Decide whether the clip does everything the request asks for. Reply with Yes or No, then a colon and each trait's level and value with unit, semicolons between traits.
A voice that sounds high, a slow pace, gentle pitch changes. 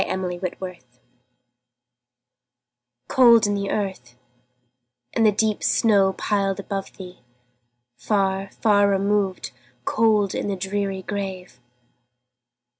Yes: high, 195 Hz; slow, 105 wpm; narrow, 1.5 semitones